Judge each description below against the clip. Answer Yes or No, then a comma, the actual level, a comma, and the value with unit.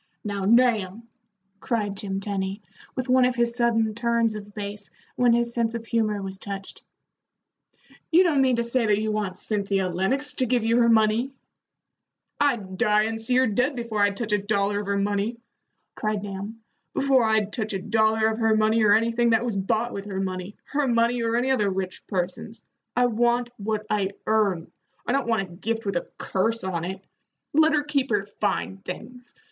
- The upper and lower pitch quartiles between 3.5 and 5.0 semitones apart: No, average, 2.9 semitones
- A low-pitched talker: No, high, 220 Hz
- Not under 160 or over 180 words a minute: No, average, 195 wpm